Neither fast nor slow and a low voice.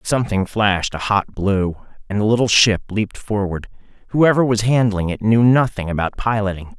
Yes: average, 170 wpm; low, 105 Hz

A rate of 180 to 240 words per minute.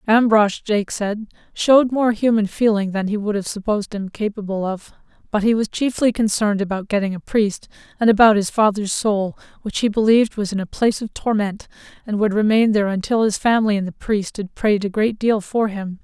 Yes: fast, 205 wpm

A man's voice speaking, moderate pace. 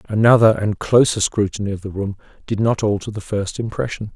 Yes: male; average, 190 wpm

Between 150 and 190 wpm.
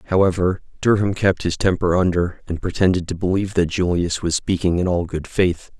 Yes: average, 185 wpm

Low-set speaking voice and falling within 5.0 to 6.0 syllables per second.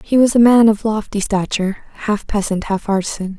No: high, 210 Hz; 5.5 syllables/s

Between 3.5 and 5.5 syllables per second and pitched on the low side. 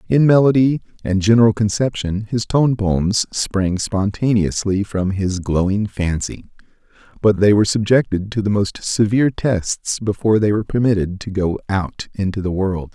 Yes: 4.8 syllables/s; low, 105 Hz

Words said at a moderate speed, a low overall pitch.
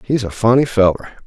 Yes: average, 190 wpm; low, 115 Hz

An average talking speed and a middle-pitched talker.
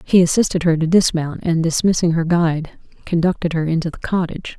Yes: average, 185 wpm; medium, 170 Hz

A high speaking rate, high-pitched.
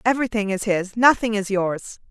No: average, 170 wpm; high, 210 Hz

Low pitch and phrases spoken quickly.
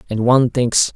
No: low, 120 Hz; average, 190 wpm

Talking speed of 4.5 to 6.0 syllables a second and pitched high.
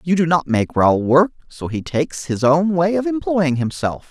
No: 4.7 syllables/s; medium, 160 Hz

